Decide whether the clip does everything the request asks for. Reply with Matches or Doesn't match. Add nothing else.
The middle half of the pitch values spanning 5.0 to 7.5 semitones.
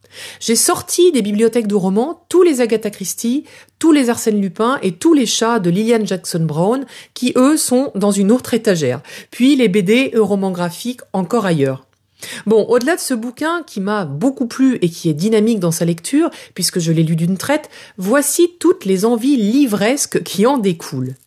Matches